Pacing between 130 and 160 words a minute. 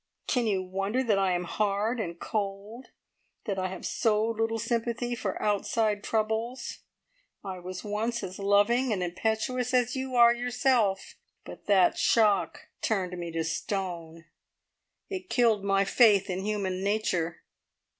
Yes: average, 145 wpm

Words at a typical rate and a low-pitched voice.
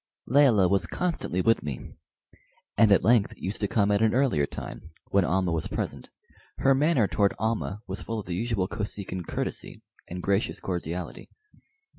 Yes: average, 165 wpm; low, 100 Hz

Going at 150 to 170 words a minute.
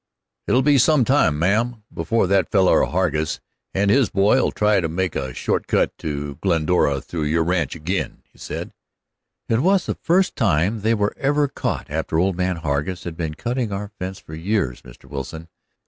No: average, 180 wpm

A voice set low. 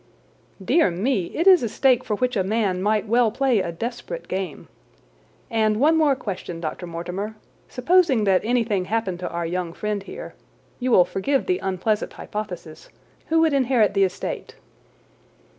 No: high, 215 Hz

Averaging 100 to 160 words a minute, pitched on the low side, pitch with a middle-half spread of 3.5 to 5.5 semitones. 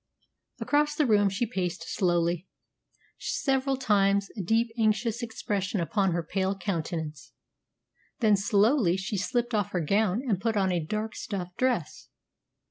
No: average, 140 wpm; high, 200 Hz; average, 4.0 semitones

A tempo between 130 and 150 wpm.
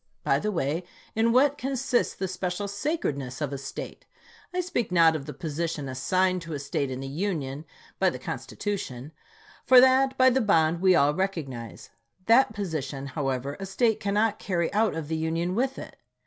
No: average, 185 wpm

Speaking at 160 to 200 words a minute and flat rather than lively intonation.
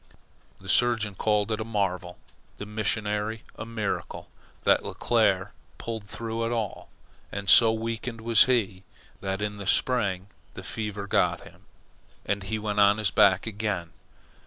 No: average, 150 wpm; narrow, 2.0 semitones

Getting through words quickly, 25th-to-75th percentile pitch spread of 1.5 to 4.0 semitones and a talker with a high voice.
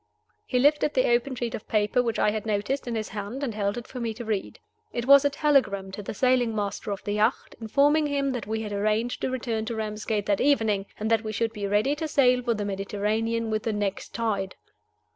Yes: fast, 235 wpm; average, 3.3 semitones; high, 225 Hz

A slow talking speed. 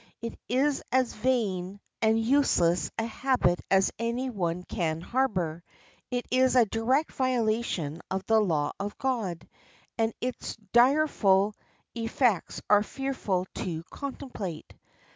Yes: slow, 125 wpm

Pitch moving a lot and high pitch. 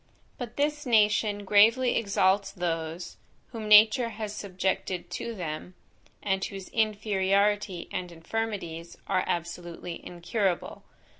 No: average, 3.4 semitones; high, 200 Hz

